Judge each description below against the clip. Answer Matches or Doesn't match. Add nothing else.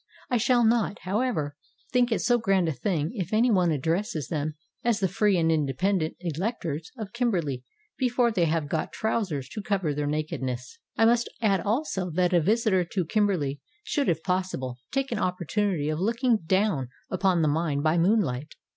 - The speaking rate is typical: Matches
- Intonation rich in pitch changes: Matches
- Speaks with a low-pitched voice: Doesn't match